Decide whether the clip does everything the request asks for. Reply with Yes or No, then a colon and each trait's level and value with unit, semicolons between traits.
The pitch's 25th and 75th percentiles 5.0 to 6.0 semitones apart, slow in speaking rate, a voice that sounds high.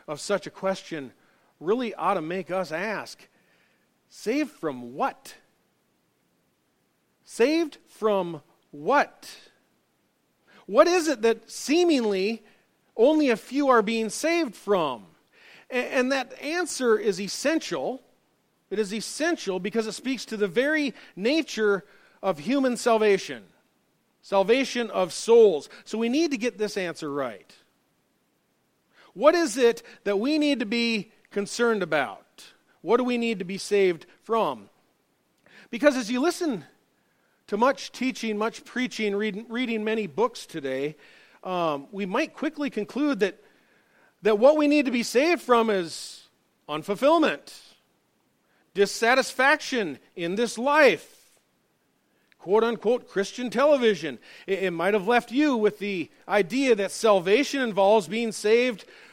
Yes: average, 5.3 semitones; slow, 130 wpm; high, 230 Hz